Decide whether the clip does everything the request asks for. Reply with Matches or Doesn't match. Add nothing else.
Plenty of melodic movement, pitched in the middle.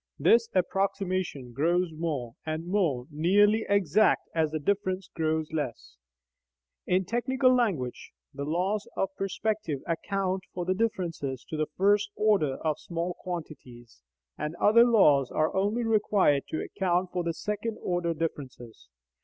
Doesn't match